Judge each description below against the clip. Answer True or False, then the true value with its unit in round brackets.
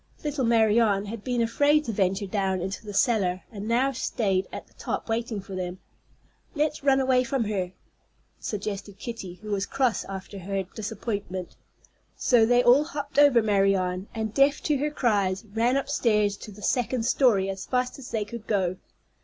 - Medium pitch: False (220 Hz)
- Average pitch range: True (4.2 semitones)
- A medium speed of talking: True (175 wpm)